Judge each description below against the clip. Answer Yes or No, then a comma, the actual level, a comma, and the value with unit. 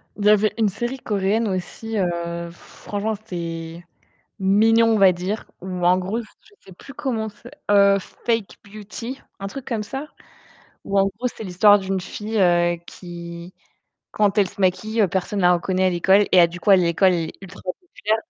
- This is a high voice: Yes, high, 195 Hz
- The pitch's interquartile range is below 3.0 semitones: No, average, 3.4 semitones